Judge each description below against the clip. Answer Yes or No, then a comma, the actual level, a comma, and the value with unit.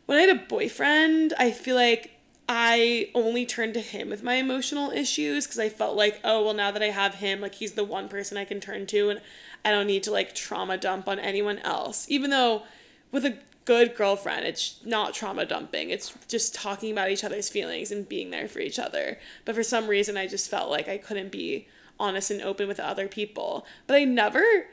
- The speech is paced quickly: Yes, fast, 220 wpm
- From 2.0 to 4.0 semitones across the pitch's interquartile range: Yes, average, 3.6 semitones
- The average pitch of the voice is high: Yes, high, 215 Hz